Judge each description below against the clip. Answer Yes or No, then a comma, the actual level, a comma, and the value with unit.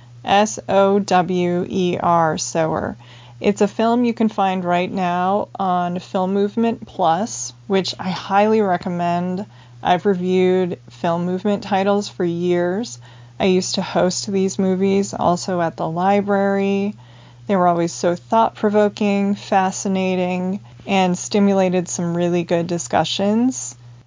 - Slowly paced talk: Yes, slow, 130 wpm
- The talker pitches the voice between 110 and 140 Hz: No, medium, 185 Hz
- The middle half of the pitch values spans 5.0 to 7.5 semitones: No, narrow, 2.4 semitones